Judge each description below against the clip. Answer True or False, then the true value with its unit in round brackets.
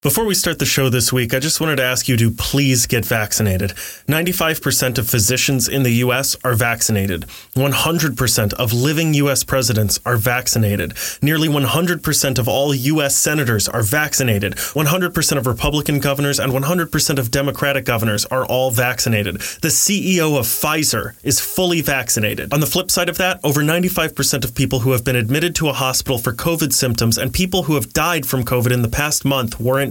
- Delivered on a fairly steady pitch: False (4.0 semitones)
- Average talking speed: True (185 wpm)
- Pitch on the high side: False (135 Hz)